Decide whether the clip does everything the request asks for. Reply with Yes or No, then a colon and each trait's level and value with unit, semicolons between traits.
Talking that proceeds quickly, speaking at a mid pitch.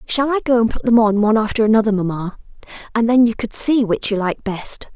No: fast, 240 wpm; high, 220 Hz